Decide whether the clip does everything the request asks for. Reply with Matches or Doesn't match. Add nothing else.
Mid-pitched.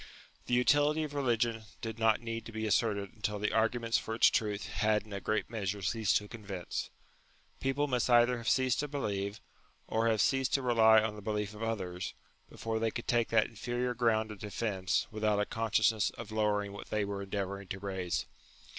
Doesn't match